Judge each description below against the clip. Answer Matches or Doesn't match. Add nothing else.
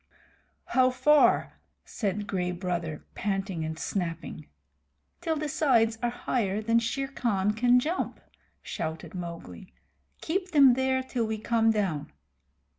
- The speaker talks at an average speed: Doesn't match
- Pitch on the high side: Matches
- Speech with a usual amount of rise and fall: Doesn't match